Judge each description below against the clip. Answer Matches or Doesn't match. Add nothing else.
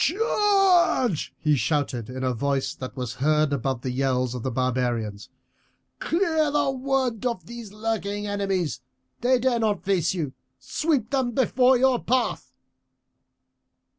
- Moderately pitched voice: Doesn't match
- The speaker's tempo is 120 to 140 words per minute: Matches